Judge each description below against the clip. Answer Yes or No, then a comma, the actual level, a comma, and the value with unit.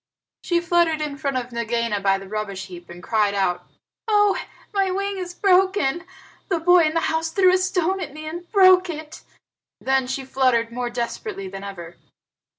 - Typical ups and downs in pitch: No, wide, 7.9 semitones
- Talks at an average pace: Yes, average, 180 wpm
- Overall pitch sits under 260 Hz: No, very high, 300 Hz